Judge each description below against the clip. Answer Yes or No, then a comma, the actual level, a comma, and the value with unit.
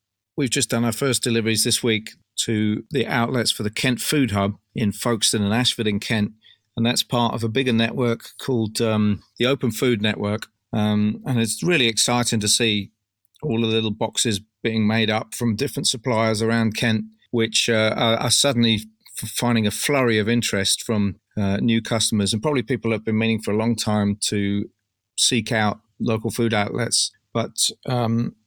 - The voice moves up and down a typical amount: No, narrow, 2.0 semitones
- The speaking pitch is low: Yes, low, 115 Hz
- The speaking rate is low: No, average, 180 wpm